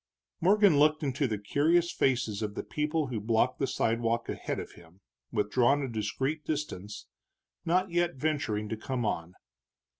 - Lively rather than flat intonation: Yes, wide, 6.2 semitones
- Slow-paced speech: No, average, 155 wpm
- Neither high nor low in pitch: No, low, 130 Hz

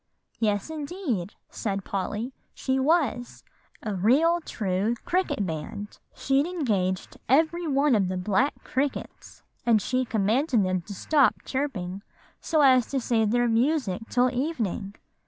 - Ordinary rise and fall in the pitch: No, wide, 5.9 semitones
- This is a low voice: No, high, 240 Hz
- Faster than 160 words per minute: No, slow, 135 wpm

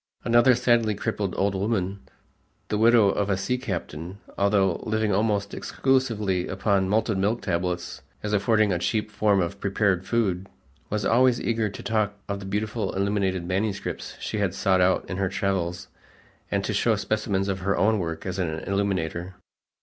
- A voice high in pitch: No, low, 100 Hz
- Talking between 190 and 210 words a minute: No, average, 165 wpm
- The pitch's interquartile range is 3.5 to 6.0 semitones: No, narrow, 2.4 semitones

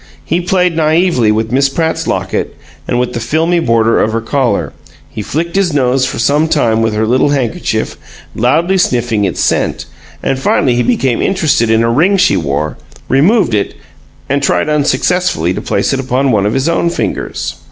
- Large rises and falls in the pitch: Yes, wide, 6.2 semitones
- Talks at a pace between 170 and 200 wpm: Yes, average, 185 wpm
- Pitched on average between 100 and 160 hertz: Yes, low, 135 Hz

